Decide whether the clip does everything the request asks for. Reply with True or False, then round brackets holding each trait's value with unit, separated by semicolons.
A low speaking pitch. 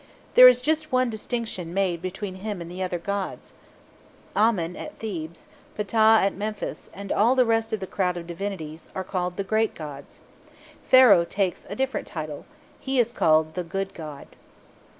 False (195 Hz)